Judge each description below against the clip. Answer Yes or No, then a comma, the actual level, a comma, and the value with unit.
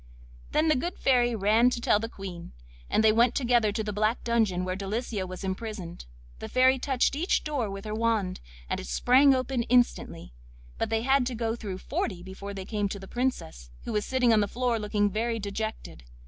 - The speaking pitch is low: No, high, 220 Hz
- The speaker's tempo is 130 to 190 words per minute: No, fast, 205 wpm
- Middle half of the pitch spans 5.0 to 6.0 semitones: No, average, 3.7 semitones